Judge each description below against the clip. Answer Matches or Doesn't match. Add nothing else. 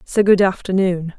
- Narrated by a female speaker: Matches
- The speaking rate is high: Doesn't match